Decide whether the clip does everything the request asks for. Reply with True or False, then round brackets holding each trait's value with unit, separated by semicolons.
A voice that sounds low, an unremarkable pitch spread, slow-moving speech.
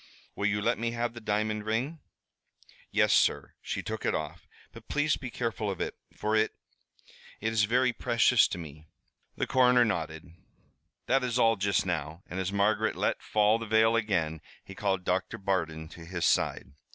False (105 Hz; 4.3 semitones; 180 wpm)